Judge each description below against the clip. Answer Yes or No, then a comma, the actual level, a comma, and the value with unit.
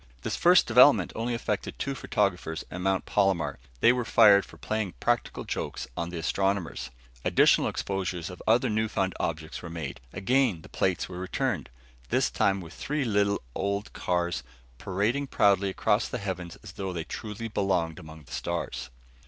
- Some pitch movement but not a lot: Yes, average, 3.8 semitones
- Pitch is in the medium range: No, very low, 95 Hz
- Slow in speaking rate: No, average, 165 wpm